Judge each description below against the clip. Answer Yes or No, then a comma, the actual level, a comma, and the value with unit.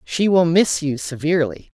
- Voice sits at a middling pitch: Yes, medium, 160 Hz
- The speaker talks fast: No, average, 165 wpm